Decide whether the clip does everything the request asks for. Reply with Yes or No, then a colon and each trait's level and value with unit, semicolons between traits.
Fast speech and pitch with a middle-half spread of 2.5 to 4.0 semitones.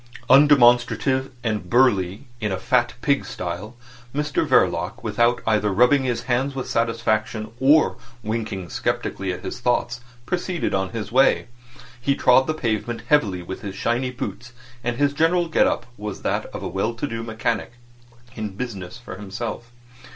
No: average, 160 wpm; average, 3.6 semitones